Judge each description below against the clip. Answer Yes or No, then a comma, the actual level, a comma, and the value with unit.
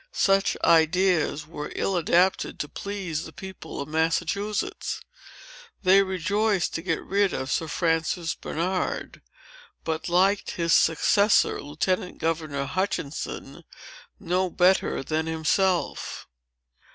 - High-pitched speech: No, medium, 175 Hz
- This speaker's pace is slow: Yes, slow, 110 wpm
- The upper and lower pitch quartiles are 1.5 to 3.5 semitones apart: Yes, average, 3.0 semitones